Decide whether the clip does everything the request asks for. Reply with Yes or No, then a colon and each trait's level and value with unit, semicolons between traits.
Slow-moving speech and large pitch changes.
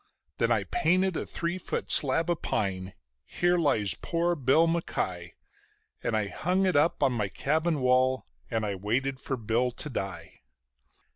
No: average, 160 wpm; wide, 7.5 semitones